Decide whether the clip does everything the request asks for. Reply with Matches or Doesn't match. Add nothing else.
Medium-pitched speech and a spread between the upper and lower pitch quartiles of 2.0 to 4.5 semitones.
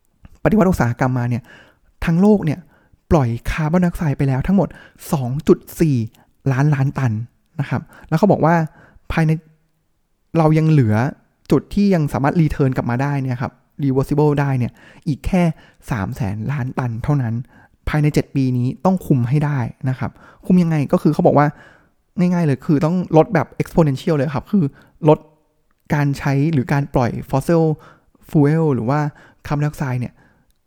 Matches